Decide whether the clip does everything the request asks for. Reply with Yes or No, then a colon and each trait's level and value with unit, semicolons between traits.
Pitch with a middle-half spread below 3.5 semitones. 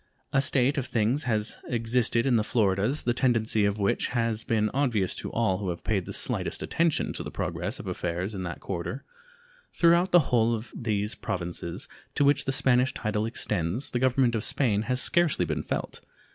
No: average, 4.0 semitones